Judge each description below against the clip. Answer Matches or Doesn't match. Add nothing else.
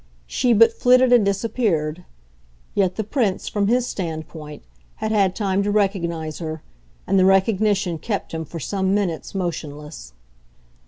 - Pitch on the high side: Matches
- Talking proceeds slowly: Doesn't match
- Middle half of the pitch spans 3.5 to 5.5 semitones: Matches